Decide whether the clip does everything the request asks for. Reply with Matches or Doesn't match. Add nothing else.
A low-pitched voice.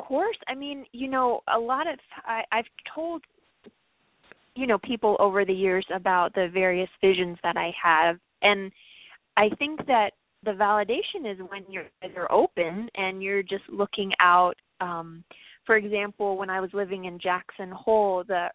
Doesn't match